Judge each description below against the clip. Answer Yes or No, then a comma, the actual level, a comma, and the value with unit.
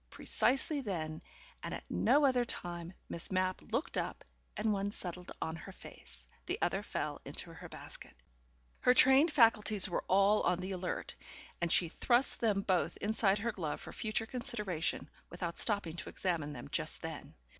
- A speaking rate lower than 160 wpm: No, average, 165 wpm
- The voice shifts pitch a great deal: No, average, 4.6 semitones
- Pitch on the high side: Yes, high, 195 Hz